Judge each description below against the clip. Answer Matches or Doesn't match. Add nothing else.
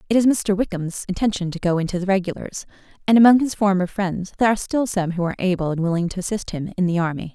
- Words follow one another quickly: Matches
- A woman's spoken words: Matches